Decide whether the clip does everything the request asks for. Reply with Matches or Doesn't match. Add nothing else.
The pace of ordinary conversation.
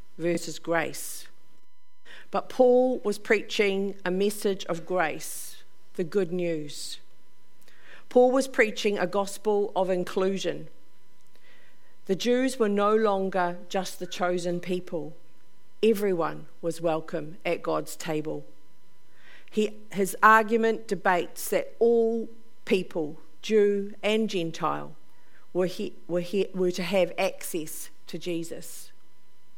Doesn't match